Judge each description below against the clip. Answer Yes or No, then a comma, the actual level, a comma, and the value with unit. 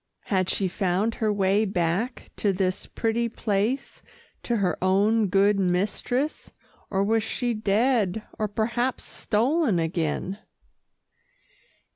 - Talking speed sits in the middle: No, slow, 115 wpm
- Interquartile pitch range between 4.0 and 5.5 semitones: No, average, 3.2 semitones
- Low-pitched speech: No, high, 205 Hz